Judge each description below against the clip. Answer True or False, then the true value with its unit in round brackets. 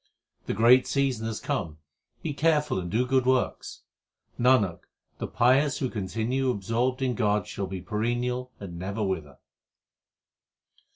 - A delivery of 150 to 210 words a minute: False (135 wpm)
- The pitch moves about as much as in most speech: True (4.5 semitones)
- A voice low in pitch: True (120 Hz)